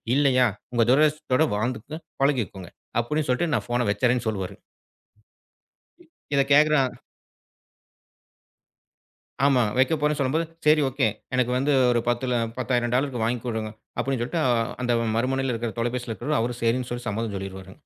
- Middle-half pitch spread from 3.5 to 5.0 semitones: No, average, 3.1 semitones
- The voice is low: Yes, low, 125 Hz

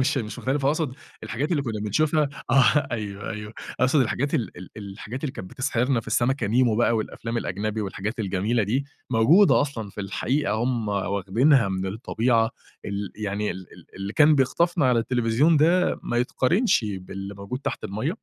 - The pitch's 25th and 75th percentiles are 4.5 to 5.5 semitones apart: Yes, average, 4.8 semitones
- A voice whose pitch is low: Yes, low, 115 Hz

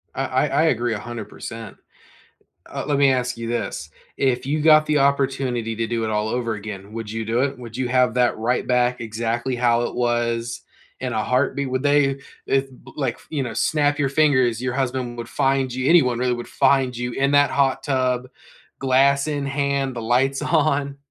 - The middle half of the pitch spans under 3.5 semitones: Yes, average, 2.7 semitones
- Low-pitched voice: Yes, low, 125 Hz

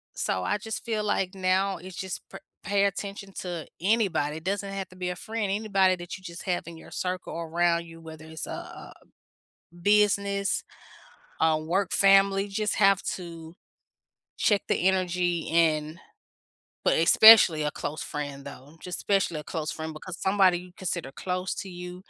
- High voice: No, medium, 180 Hz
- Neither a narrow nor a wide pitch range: Yes, average, 3.1 semitones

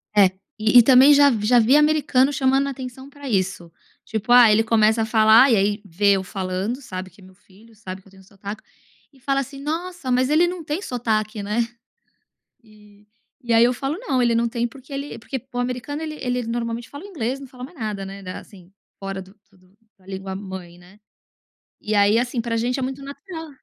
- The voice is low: No, high, 230 Hz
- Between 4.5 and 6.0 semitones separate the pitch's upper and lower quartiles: Yes, average, 4.9 semitones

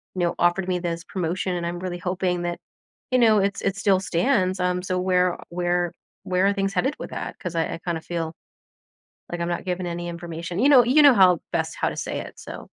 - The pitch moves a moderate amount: No, narrow, 1.9 semitones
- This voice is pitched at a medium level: Yes, medium, 180 Hz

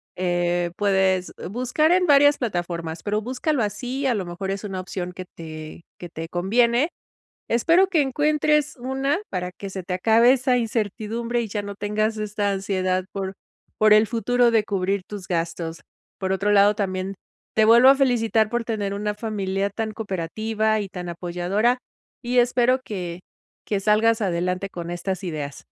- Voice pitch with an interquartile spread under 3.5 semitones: No, average, 4.3 semitones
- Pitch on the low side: No, high, 205 Hz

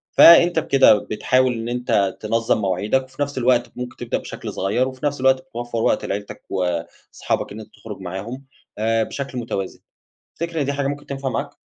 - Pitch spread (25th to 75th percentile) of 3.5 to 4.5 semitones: Yes, average, 4.2 semitones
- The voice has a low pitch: Yes, low, 125 Hz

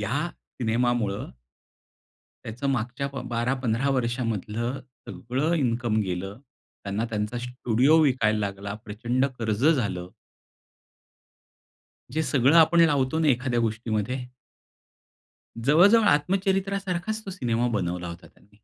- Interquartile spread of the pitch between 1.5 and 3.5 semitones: No, average, 5.1 semitones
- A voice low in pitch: Yes, low, 120 Hz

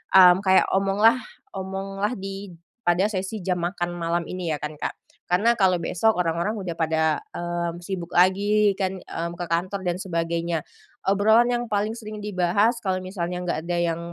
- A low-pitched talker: No, medium, 185 Hz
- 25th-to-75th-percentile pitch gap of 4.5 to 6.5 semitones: No, average, 2.7 semitones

